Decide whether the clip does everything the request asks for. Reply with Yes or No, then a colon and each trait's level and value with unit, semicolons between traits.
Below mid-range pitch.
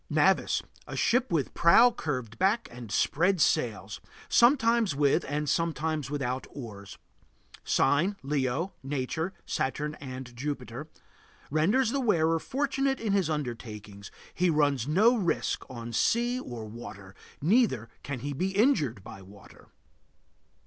No: medium, 150 Hz